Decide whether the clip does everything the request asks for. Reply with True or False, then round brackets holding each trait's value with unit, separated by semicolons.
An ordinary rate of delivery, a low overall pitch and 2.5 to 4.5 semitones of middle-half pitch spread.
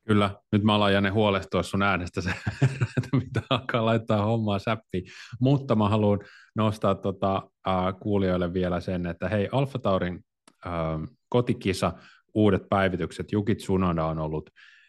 True (140 wpm; 100 Hz; 3.1 semitones)